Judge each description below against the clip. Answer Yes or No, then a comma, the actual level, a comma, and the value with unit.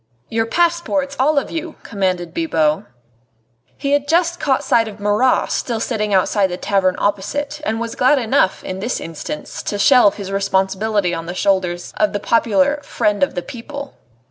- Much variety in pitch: Yes, wide, 6.6 semitones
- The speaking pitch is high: Yes, high, 220 Hz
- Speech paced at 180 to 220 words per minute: No, average, 170 wpm